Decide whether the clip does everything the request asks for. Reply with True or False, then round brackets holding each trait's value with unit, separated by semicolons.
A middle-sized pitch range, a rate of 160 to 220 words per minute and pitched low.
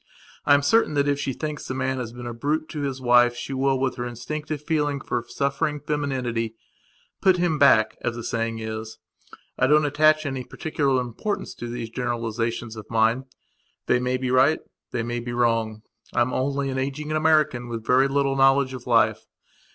True (3.2 semitones; 190 wpm; 130 Hz)